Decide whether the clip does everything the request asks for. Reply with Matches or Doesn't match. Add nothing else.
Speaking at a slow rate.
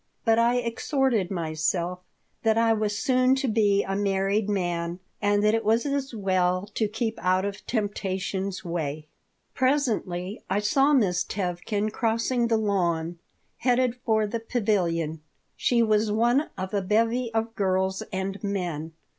Doesn't match